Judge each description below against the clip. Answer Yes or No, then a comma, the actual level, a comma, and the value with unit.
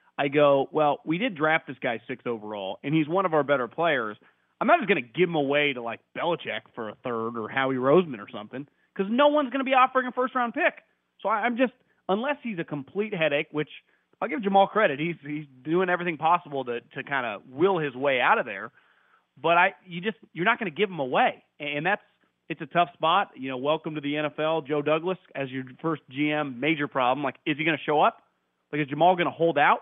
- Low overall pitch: No, medium, 160 Hz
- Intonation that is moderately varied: Yes, average, 5.0 semitones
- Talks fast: Yes, fast, 235 wpm